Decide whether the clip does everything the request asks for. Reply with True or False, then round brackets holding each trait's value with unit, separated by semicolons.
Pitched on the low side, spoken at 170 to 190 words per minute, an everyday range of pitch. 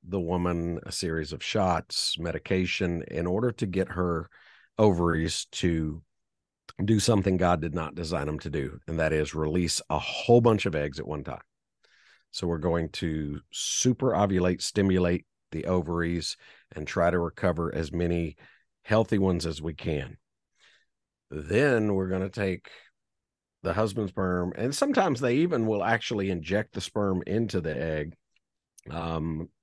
False (90 Hz; 155 wpm; 3.3 semitones)